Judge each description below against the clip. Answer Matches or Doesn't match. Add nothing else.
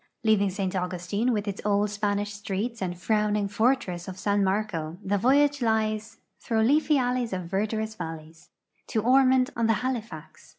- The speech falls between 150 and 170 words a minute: Matches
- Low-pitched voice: Doesn't match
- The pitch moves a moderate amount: Matches